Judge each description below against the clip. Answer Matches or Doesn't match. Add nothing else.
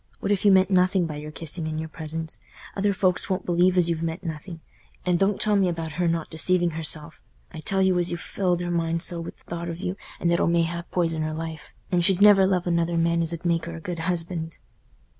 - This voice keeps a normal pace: Doesn't match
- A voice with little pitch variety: Matches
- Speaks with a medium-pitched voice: Matches